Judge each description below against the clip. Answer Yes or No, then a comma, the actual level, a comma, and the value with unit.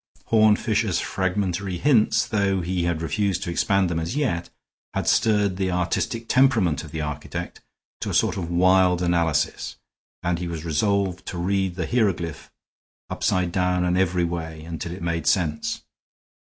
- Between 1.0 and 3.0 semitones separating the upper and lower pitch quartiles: Yes, average, 2.7 semitones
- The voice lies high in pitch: No, very low, 90 Hz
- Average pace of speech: Yes, average, 160 wpm